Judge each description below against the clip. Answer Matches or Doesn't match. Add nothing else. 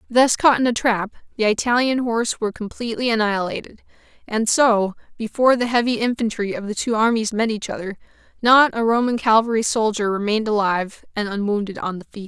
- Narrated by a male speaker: Doesn't match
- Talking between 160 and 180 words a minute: Matches